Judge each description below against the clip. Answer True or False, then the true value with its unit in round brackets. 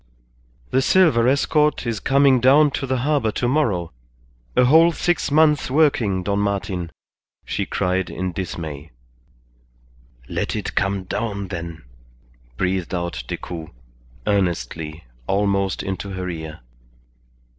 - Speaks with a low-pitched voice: True (100 Hz)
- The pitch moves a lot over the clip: True (7.0 semitones)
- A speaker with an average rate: False (115 wpm)